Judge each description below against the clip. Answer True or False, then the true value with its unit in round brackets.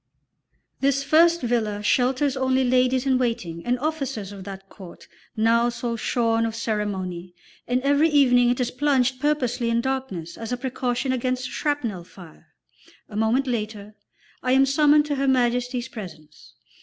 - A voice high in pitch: True (245 Hz)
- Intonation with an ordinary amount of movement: True (3.4 semitones)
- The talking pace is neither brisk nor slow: True (155 wpm)